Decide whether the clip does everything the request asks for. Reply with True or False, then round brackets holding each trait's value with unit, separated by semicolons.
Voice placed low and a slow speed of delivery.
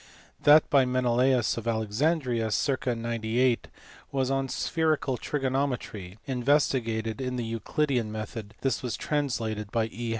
True (125 Hz; 125 wpm)